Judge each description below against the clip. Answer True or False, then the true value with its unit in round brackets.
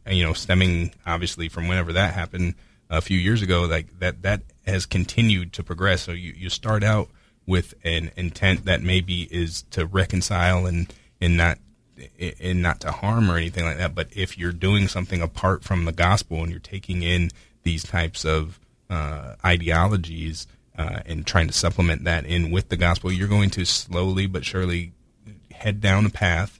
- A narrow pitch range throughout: True (2.1 semitones)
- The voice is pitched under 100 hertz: True (90 Hz)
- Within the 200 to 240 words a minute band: False (185 wpm)